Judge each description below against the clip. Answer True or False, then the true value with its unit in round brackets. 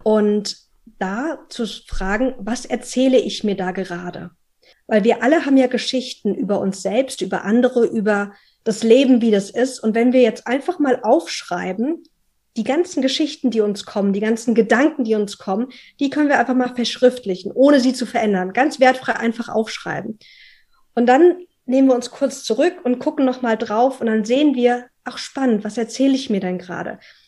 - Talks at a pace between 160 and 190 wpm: True (185 wpm)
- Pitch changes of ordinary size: True (3.5 semitones)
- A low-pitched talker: False (240 Hz)